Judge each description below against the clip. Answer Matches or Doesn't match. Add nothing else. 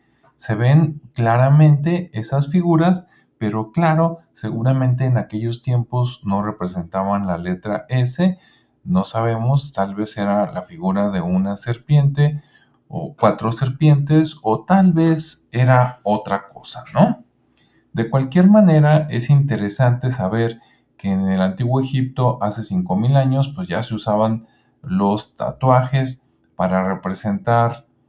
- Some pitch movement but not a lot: Doesn't match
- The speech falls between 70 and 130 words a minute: Matches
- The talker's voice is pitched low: Matches